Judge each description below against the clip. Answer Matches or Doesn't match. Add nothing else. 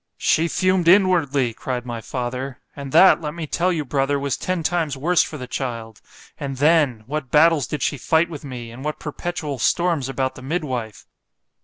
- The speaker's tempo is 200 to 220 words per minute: Doesn't match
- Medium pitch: Matches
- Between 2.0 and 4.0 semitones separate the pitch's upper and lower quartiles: Doesn't match